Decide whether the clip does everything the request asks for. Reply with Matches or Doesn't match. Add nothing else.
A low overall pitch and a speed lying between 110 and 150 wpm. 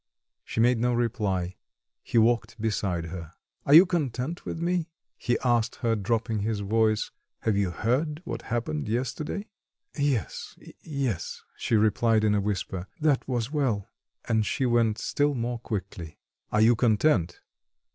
Matches